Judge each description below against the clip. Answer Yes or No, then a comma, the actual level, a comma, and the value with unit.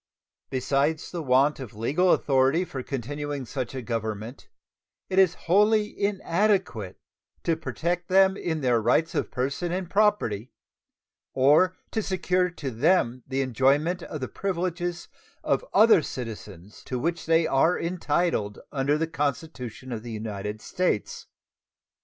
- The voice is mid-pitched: Yes, medium, 145 Hz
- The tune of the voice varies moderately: No, wide, 5.9 semitones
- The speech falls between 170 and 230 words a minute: No, slow, 135 wpm